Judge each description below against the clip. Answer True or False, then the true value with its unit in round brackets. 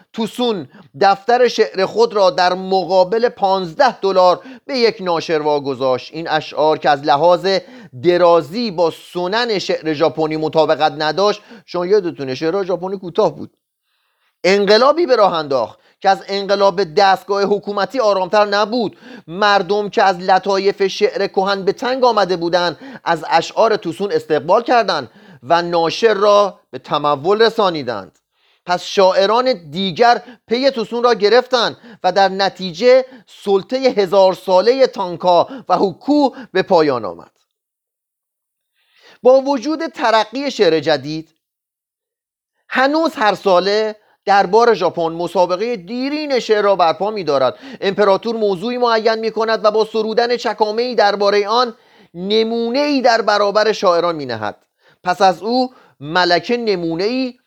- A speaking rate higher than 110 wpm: True (130 wpm)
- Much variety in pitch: False (4.6 semitones)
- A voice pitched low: False (200 Hz)